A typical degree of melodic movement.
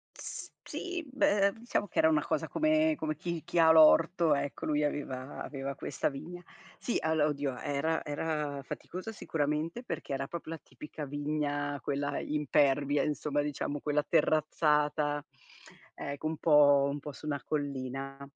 No: narrow, 2.1 semitones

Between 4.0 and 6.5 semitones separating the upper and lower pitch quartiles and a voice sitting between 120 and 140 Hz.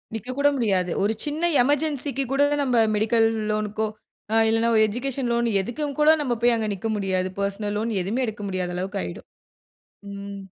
No: average, 4.6 semitones; high, 225 Hz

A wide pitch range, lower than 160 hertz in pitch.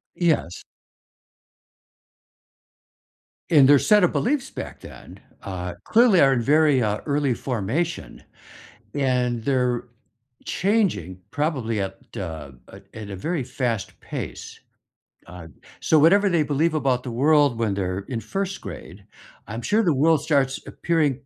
Yes: wide, 6.3 semitones; low, 135 Hz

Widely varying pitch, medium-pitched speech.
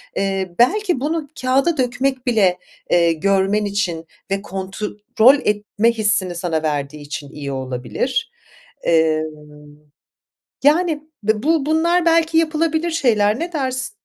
No: wide, 8.8 semitones; high, 220 Hz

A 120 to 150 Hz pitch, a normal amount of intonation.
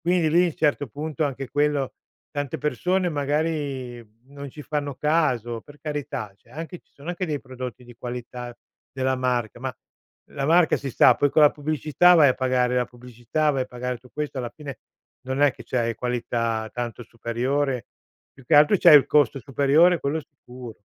Yes: medium, 140 Hz; average, 3.4 semitones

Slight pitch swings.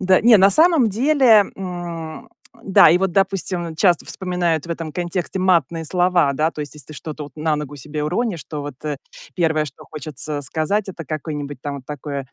No: average, 4.0 semitones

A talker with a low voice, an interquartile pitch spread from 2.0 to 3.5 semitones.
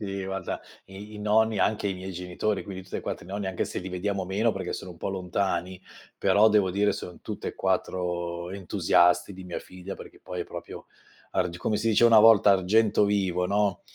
Yes: very low, 95 Hz; narrow, 2.3 semitones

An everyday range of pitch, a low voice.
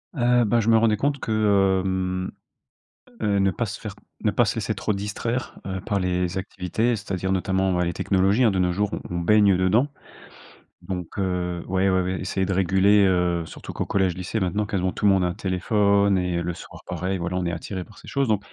No: narrow, 2.3 semitones; very low, 95 Hz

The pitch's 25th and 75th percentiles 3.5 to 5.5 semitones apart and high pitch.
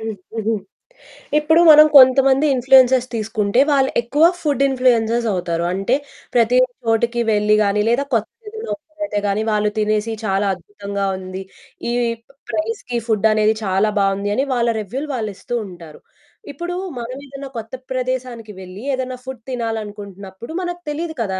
Yes: average, 4.1 semitones; high, 230 Hz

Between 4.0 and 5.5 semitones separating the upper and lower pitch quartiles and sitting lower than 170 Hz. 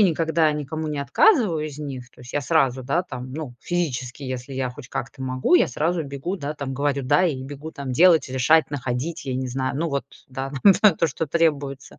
No: average, 3.6 semitones; medium, 140 Hz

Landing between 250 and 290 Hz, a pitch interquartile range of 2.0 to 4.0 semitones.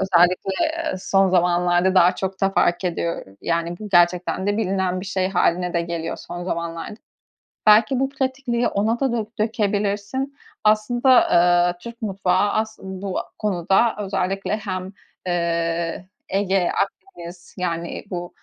No: high, 190 Hz; average, 3.3 semitones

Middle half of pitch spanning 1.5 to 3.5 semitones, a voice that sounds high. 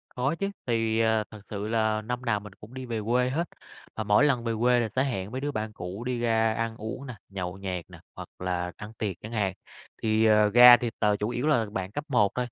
No: average, 2.8 semitones; low, 110 Hz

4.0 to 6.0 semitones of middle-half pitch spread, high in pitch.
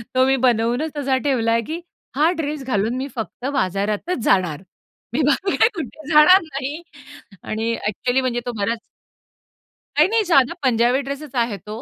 Yes: average, 4.7 semitones; very high, 260 Hz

